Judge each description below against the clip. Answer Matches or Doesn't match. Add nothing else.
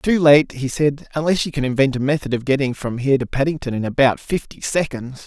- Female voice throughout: Doesn't match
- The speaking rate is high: Matches